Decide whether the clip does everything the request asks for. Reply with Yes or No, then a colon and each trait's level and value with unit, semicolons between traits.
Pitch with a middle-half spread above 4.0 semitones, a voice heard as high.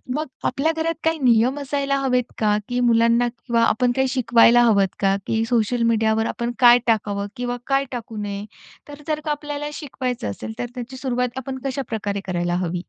No: average, 3.3 semitones; high, 245 Hz